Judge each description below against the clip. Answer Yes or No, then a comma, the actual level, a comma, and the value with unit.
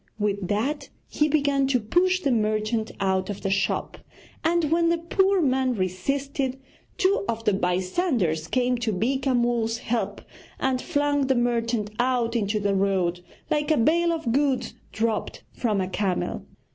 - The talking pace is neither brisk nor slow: Yes, average, 160 wpm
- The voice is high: Yes, high, 240 Hz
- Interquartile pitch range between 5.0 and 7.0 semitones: Yes, wide, 5.6 semitones